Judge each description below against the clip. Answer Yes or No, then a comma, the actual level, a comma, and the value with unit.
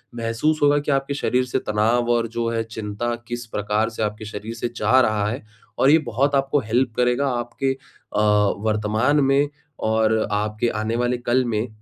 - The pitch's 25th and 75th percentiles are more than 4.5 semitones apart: No, average, 3.0 semitones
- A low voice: Yes, low, 120 Hz